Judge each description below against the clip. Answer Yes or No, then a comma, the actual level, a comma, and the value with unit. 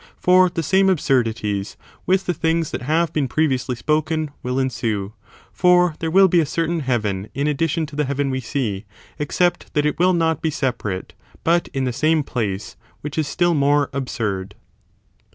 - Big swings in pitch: No, average, 4.7 semitones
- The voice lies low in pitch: No, medium, 145 Hz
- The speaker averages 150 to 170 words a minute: No, average, 180 wpm